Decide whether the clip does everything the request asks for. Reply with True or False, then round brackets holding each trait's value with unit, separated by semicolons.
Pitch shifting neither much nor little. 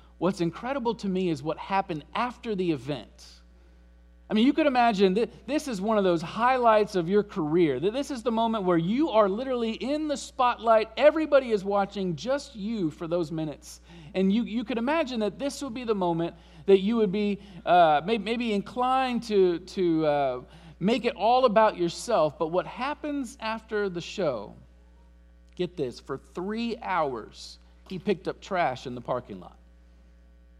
False (6.2 semitones)